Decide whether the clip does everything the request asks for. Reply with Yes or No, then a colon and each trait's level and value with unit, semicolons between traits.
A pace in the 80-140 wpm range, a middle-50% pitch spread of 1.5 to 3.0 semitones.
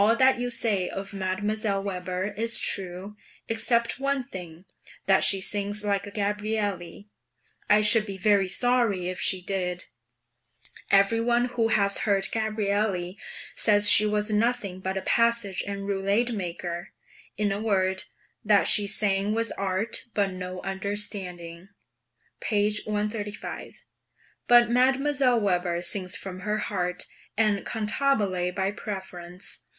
Yes: slow, 135 wpm; narrow, 2.5 semitones